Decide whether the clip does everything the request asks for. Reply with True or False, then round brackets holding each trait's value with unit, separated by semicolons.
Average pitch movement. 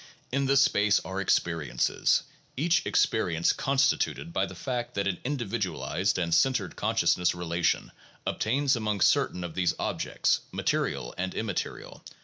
False (6.7 semitones)